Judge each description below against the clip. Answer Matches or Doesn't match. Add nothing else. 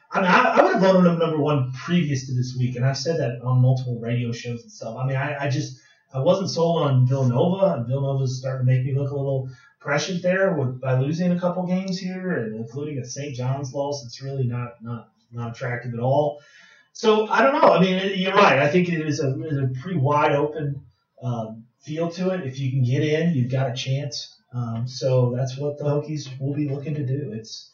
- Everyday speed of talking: Doesn't match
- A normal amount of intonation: Matches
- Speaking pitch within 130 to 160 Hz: Matches